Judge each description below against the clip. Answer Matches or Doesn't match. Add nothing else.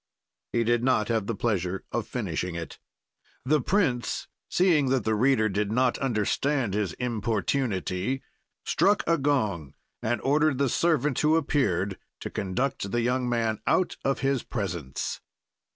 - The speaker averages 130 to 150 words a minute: Matches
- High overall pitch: Doesn't match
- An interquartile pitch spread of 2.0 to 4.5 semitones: Doesn't match